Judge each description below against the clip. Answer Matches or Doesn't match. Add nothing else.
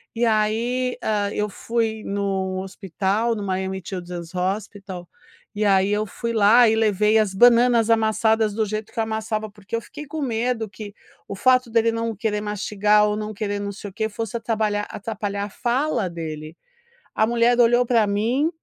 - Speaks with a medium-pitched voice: Doesn't match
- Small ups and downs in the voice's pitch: Matches